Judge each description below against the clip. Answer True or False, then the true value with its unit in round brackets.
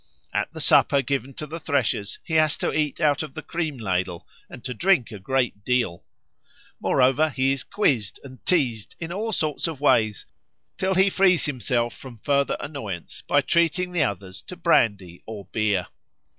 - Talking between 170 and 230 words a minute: True (175 wpm)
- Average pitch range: False (6.1 semitones)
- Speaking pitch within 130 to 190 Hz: True (135 Hz)